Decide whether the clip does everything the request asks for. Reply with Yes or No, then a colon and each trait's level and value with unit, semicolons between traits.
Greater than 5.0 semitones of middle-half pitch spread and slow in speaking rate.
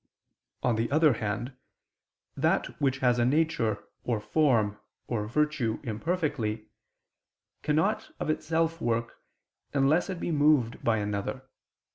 Yes: wide, 5.6 semitones; slow, 120 wpm